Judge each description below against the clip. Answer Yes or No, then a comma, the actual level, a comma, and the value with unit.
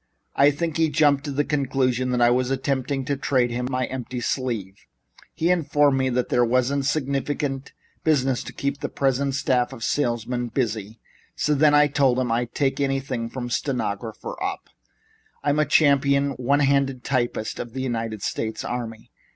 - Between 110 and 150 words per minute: No, average, 170 wpm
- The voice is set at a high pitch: No, low, 130 Hz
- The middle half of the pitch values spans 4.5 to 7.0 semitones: No, narrow, 2.5 semitones